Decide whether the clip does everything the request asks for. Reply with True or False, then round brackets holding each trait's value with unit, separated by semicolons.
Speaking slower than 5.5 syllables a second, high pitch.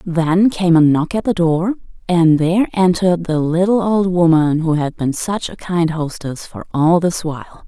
False (4.6 syllables/s; 170 Hz)